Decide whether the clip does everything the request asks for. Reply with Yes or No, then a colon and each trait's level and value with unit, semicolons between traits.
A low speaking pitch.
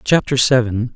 Yes: low, 125 Hz